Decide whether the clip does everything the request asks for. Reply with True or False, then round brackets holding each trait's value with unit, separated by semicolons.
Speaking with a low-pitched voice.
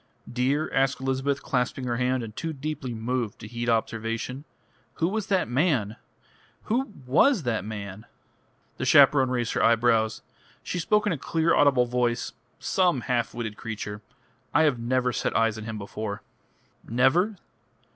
True (125 Hz)